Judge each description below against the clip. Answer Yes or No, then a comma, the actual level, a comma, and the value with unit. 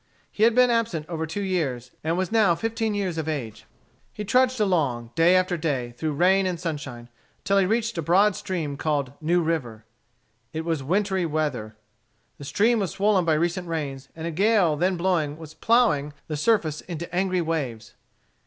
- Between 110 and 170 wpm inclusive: No, average, 180 wpm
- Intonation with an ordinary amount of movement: Yes, average, 4.5 semitones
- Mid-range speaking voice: Yes, medium, 170 Hz